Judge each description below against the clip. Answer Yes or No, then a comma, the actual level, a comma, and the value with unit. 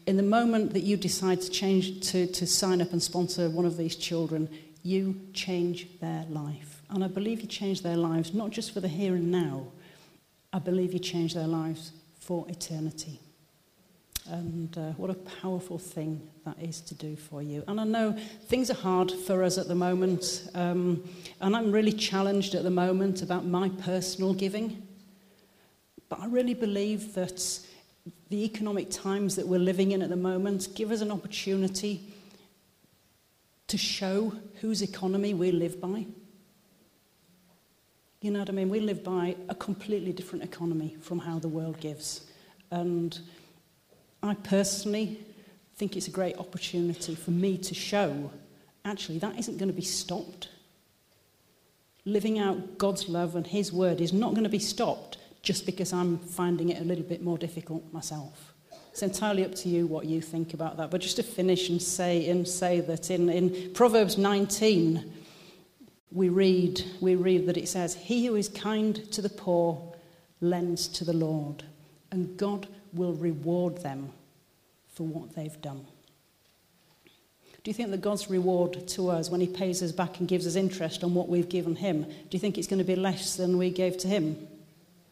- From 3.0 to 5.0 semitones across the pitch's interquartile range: No, narrow, 2.4 semitones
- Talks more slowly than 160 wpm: No, average, 175 wpm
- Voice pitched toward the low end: No, medium, 180 Hz